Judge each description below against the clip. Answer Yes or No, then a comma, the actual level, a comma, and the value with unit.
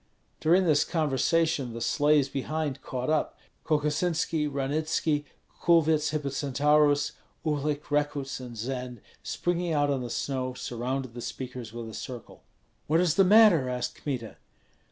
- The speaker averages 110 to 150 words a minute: Yes, slow, 135 wpm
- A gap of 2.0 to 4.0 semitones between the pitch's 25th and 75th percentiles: Yes, average, 3.4 semitones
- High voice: No, medium, 145 Hz